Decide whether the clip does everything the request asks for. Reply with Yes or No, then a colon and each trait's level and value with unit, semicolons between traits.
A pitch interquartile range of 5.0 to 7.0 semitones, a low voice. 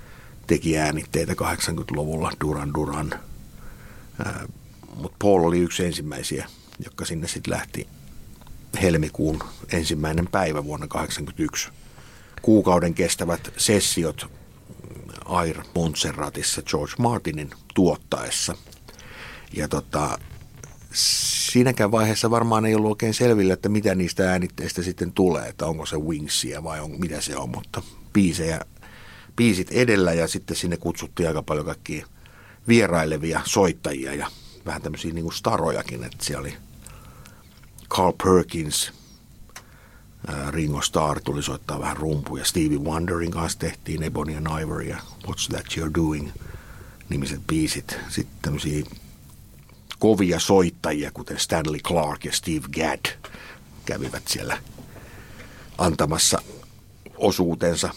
Yes: wide, 5.4 semitones; very low, 85 Hz